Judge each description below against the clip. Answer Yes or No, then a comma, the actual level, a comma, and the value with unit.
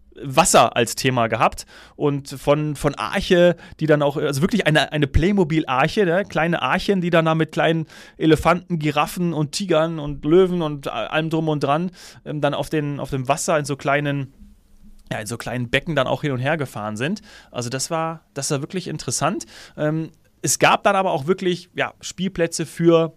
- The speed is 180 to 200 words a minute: Yes, average, 185 wpm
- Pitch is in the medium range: Yes, medium, 155 Hz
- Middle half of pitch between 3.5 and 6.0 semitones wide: No, average, 3.1 semitones